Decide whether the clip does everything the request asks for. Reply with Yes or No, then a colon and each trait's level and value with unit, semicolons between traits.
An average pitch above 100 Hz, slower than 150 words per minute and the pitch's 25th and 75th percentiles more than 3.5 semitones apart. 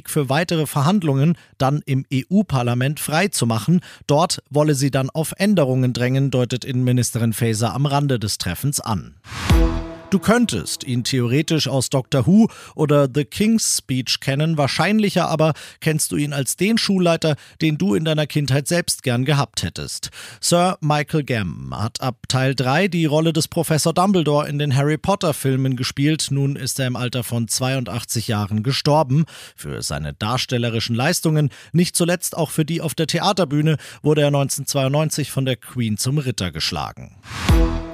No: medium, 140 Hz; average, 155 wpm; average, 4.2 semitones